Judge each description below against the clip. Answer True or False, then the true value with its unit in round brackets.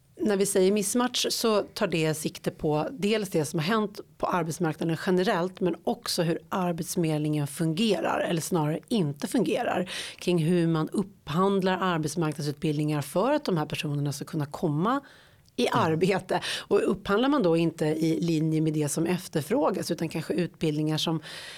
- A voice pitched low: False (170 Hz)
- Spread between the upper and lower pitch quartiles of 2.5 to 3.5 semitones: True (3.2 semitones)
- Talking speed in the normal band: True (155 wpm)